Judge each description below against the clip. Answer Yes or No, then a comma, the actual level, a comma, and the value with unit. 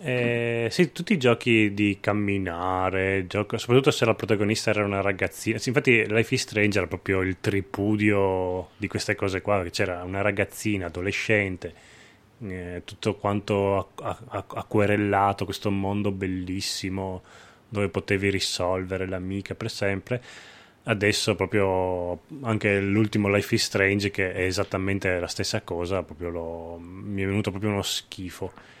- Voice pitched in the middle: No, low, 100 Hz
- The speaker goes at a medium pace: Yes, average, 140 wpm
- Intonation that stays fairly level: Yes, narrow, 2.2 semitones